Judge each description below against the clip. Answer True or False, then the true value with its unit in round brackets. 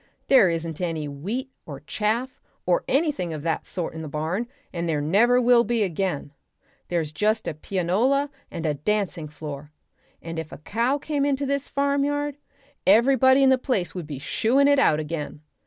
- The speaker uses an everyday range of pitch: False (8.7 semitones)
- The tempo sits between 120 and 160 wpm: False (175 wpm)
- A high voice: True (195 Hz)